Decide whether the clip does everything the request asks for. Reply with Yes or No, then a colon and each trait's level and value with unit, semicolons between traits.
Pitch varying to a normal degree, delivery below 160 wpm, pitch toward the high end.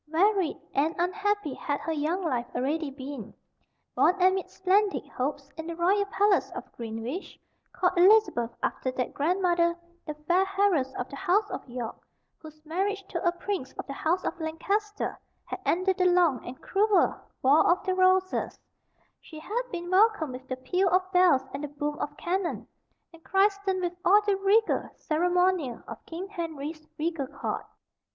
No: average, 4.5 semitones; average, 165 wpm; very high, 345 Hz